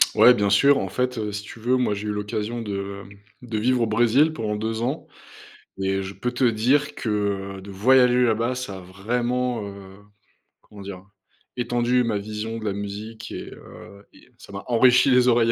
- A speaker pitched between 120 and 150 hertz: No, low, 110 Hz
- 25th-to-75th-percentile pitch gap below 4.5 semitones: Yes, average, 3.5 semitones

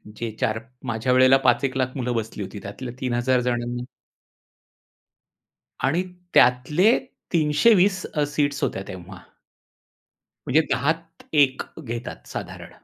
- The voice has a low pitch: Yes, low, 130 Hz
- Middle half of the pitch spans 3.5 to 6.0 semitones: Yes, average, 3.8 semitones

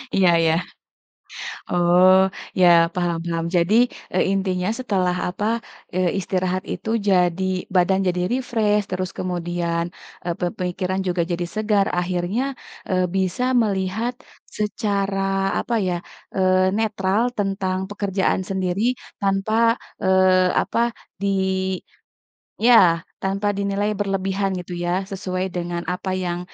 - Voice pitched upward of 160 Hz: Yes, medium, 185 Hz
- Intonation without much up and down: Yes, narrow, 1.8 semitones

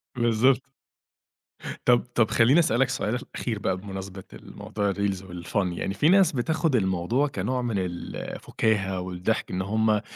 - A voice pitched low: Yes, low, 110 Hz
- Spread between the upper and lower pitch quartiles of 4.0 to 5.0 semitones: Yes, average, 4.6 semitones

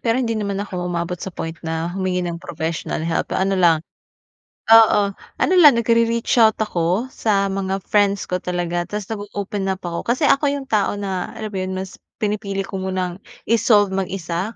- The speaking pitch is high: Yes, high, 195 Hz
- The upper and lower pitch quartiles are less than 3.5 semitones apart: Yes, average, 3.1 semitones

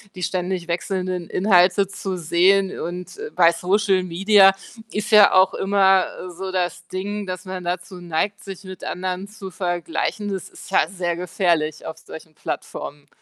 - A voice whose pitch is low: No, medium, 185 Hz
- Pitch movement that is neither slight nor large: No, narrow, 1.8 semitones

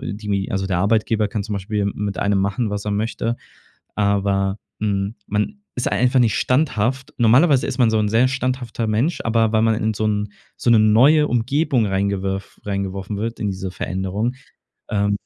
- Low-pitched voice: Yes, low, 105 Hz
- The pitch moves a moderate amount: Yes, average, 3.0 semitones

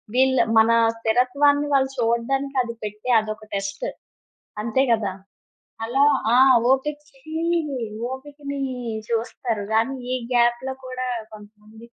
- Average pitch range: Yes, average, 3.4 semitones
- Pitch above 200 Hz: Yes, high, 245 Hz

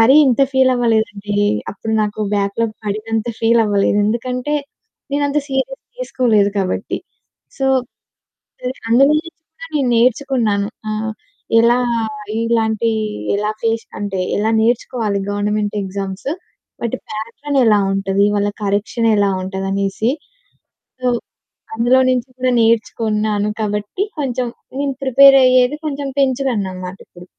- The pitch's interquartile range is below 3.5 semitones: No, average, 3.8 semitones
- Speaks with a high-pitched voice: Yes, high, 225 Hz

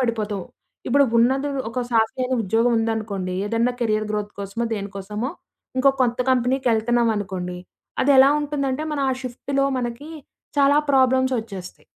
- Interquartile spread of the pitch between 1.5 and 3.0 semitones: No, average, 3.6 semitones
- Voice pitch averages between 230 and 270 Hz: Yes, high, 235 Hz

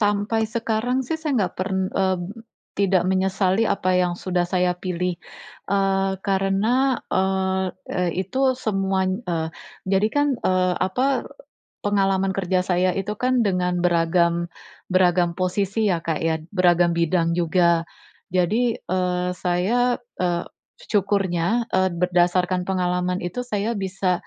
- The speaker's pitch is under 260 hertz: Yes, medium, 185 Hz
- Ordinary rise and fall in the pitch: No, narrow, 2.1 semitones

